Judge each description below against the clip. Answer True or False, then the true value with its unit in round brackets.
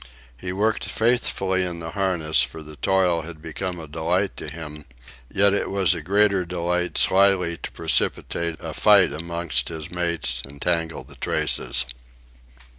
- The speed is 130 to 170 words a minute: True (155 wpm)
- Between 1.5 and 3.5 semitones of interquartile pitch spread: True (2.9 semitones)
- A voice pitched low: True (85 Hz)